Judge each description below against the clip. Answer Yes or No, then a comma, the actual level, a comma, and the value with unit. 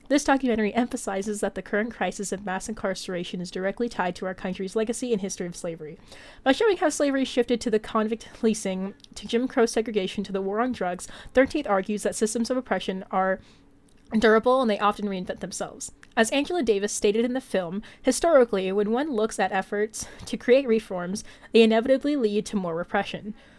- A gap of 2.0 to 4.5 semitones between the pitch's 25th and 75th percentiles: Yes, average, 3.9 semitones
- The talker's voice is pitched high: Yes, high, 215 Hz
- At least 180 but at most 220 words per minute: Yes, average, 190 wpm